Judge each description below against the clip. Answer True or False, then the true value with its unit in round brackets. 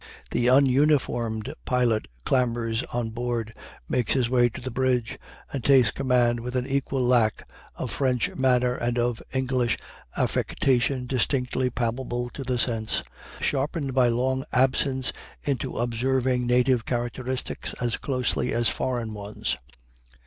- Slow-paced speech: True (130 wpm)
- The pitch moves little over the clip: True (1.7 semitones)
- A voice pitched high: False (125 Hz)